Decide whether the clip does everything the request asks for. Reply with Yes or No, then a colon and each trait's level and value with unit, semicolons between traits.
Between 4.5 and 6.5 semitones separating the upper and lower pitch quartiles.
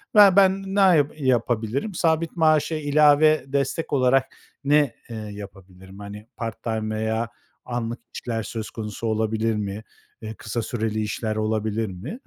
Yes: average, 5.2 semitones